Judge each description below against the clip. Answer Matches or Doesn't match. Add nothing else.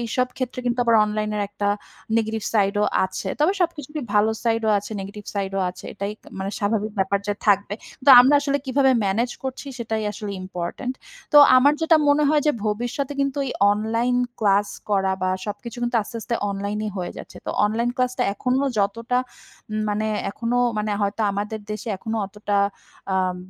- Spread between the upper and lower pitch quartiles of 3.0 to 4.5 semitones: Matches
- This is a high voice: Matches